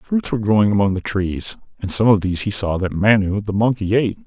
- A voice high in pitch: No, low, 105 Hz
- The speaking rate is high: Yes, fast, 240 wpm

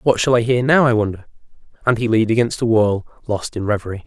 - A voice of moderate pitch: No, low, 115 Hz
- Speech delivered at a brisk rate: Yes, fast, 235 wpm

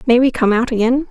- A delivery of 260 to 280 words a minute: Yes, fast, 270 wpm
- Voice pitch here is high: Yes, high, 245 Hz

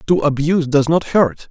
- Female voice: No, male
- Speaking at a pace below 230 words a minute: Yes, average, 200 wpm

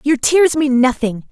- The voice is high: Yes, very high, 270 Hz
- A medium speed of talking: Yes, average, 185 wpm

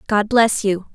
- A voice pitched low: No, high, 210 Hz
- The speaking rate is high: No, average, 190 wpm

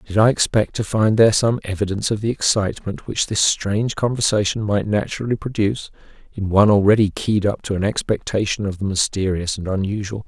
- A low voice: Yes, low, 105 Hz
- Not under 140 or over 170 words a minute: No, average, 180 wpm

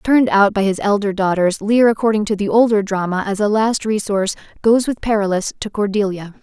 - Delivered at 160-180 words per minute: No, average, 195 wpm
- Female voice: Yes, female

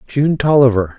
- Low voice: Yes, low, 130 Hz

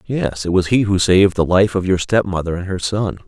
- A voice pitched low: Yes, very low, 95 Hz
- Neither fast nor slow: No, fast, 275 wpm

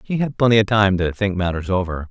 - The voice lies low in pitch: Yes, low, 100 Hz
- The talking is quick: Yes, fast, 255 wpm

